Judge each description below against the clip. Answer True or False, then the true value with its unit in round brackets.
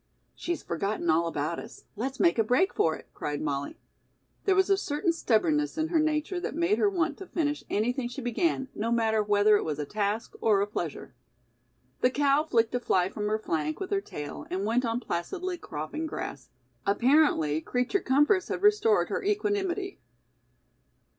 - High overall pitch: True (250 Hz)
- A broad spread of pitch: True (8.9 semitones)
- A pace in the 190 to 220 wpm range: False (180 wpm)